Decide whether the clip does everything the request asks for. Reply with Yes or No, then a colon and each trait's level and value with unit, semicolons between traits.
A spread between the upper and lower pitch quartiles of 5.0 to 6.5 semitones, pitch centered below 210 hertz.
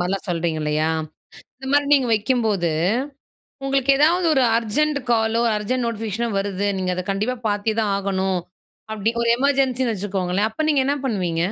No: average, 5.3 semitones; high, 220 Hz